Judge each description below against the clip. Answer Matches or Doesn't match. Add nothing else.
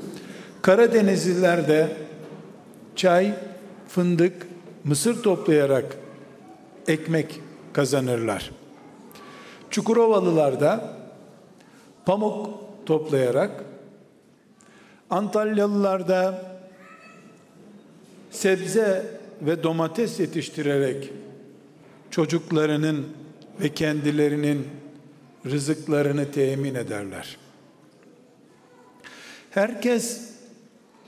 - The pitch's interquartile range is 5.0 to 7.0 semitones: Matches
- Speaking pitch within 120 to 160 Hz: Doesn't match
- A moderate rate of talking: Doesn't match